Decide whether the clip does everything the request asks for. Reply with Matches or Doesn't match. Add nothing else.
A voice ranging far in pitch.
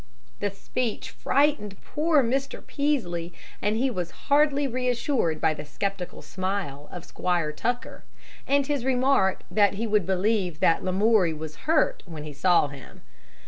Matches